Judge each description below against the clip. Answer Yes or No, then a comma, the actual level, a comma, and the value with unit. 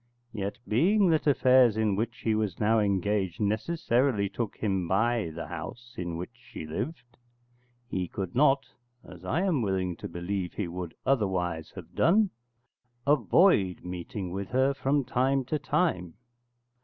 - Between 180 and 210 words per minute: No, average, 150 wpm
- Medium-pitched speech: No, low, 110 Hz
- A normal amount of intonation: No, wide, 6.3 semitones